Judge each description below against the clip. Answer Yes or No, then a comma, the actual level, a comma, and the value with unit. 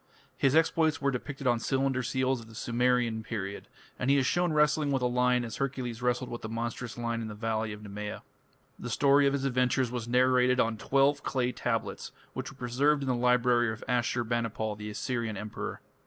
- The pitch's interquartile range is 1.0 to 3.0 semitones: Yes, average, 2.7 semitones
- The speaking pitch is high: No, low, 125 Hz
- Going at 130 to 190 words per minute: No, average, 200 wpm